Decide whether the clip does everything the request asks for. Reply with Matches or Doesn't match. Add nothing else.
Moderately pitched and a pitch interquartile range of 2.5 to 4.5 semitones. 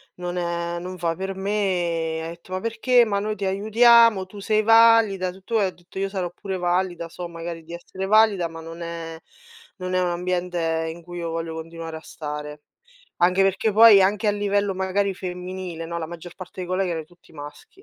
Matches